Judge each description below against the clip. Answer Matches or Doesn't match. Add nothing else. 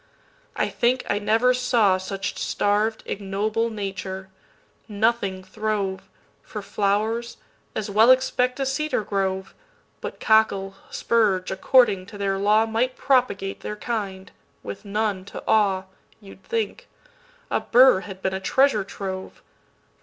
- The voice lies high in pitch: Matches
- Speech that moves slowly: Matches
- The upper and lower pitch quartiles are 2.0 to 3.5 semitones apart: Matches